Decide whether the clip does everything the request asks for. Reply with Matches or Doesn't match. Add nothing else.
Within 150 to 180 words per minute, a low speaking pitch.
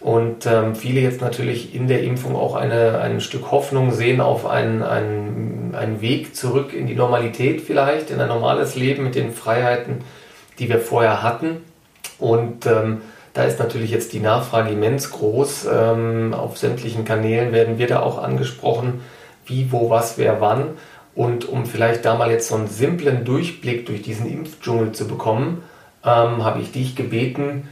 Matches